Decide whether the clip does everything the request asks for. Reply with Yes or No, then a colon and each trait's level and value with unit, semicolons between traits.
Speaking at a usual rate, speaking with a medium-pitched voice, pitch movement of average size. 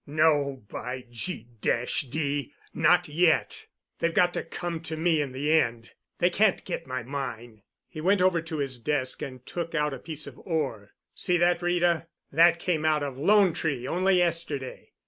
Yes: average, 170 wpm; medium, 155 Hz; average, 4.7 semitones